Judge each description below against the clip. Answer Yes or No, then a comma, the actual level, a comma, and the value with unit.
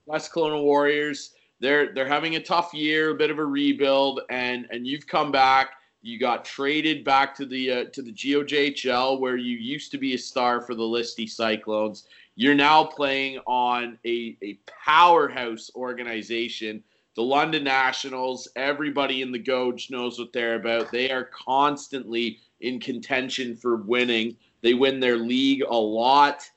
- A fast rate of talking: No, average, 165 wpm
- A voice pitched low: Yes, low, 130 Hz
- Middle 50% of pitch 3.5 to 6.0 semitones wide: No, average, 3.1 semitones